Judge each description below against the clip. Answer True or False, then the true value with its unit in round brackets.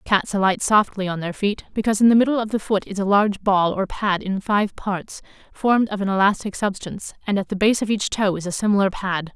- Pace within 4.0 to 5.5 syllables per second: False (5.9 syllables/s)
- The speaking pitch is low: False (200 Hz)